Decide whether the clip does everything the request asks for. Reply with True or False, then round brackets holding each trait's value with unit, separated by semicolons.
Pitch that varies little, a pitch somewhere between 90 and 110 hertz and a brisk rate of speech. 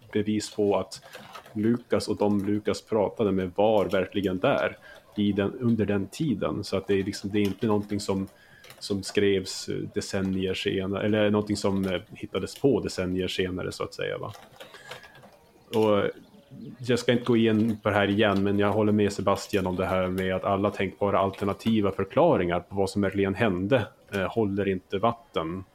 False (1.6 semitones; 100 Hz; 170 wpm)